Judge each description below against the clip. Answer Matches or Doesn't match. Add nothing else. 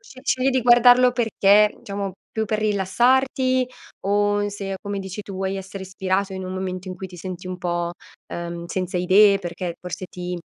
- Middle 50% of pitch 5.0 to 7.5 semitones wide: Doesn't match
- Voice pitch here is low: Doesn't match